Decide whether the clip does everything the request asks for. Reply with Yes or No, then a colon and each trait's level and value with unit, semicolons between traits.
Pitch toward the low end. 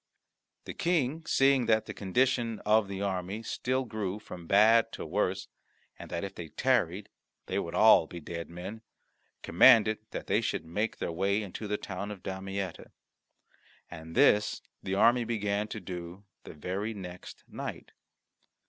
Yes: low, 100 Hz